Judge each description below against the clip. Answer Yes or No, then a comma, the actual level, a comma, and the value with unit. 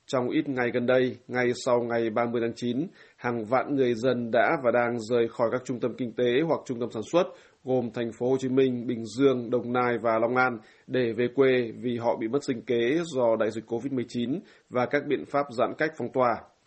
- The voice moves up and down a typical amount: No, narrow, 1.5 semitones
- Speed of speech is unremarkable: Yes, average, 230 wpm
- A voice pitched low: Yes, low, 125 Hz